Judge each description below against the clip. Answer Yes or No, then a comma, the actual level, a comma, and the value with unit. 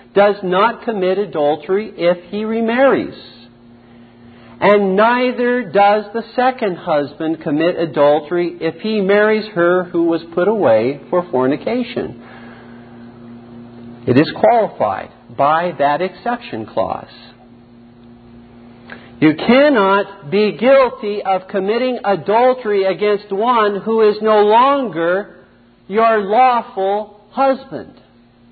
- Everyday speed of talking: No, slow, 100 wpm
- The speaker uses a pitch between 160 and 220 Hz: Yes, medium, 185 Hz